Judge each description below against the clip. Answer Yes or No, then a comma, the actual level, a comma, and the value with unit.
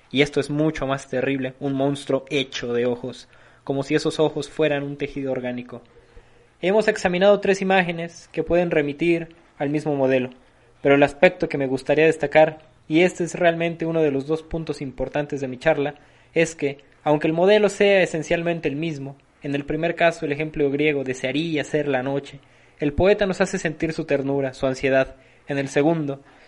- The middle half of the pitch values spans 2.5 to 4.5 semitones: Yes, average, 3.3 semitones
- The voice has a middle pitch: Yes, medium, 145 Hz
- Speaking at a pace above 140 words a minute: Yes, average, 185 wpm